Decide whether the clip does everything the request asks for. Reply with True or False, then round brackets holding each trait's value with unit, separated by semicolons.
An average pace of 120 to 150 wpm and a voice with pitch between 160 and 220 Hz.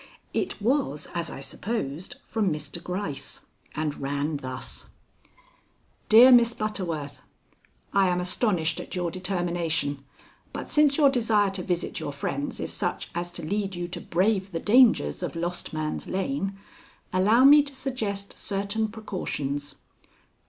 True (140 wpm; 185 Hz)